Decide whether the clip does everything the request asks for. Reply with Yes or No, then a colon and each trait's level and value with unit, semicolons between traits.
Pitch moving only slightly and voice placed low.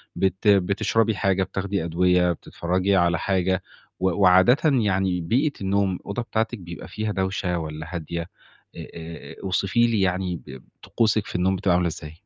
Yes: narrow, 2.3 semitones; very low, 95 Hz